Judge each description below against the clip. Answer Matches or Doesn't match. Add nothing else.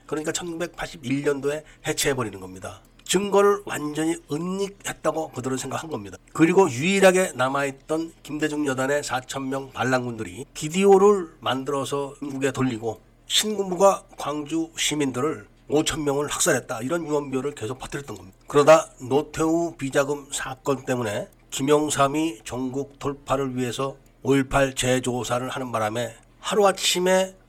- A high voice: Doesn't match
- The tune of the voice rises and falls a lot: Doesn't match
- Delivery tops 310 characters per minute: Matches